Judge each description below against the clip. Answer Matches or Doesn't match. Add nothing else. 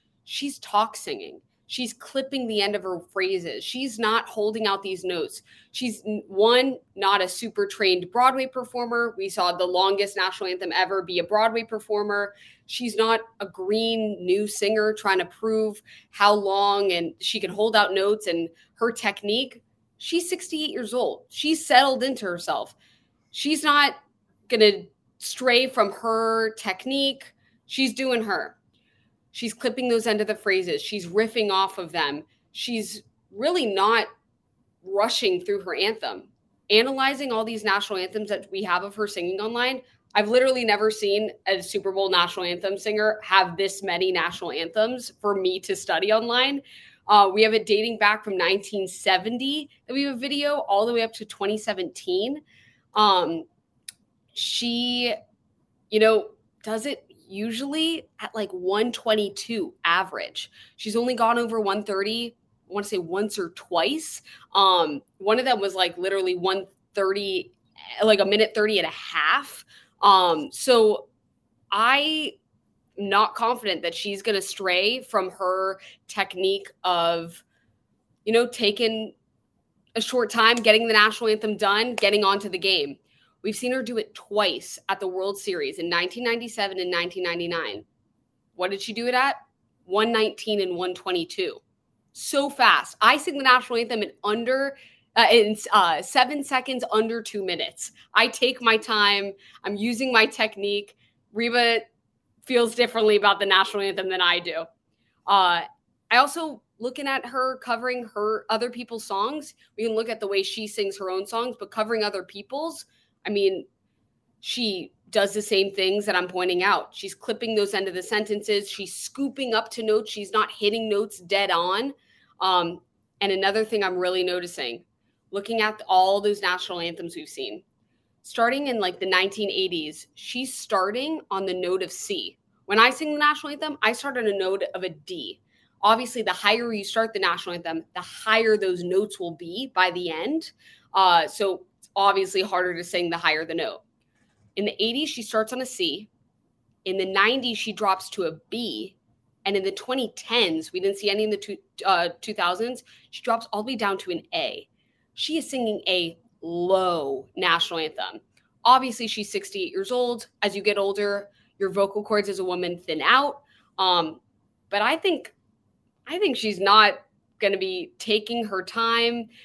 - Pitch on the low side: Doesn't match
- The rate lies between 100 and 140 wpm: Doesn't match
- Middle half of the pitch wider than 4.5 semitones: Doesn't match